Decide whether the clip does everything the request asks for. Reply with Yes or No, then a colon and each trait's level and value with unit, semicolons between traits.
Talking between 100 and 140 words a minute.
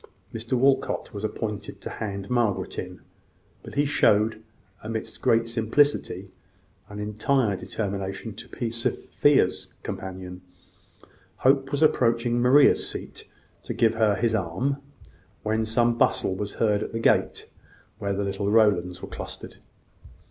Yes: slow, 135 wpm